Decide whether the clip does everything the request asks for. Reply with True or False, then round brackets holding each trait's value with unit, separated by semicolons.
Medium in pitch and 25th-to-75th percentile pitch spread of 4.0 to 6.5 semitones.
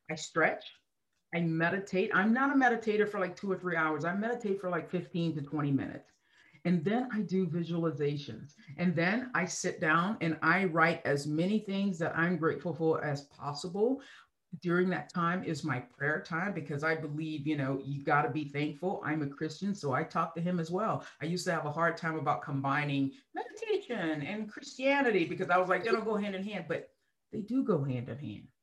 True (170 Hz; 4.3 semitones)